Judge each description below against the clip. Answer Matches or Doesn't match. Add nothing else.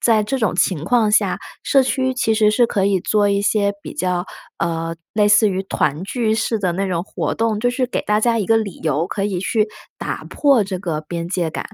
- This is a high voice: Matches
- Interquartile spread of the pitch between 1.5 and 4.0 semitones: Matches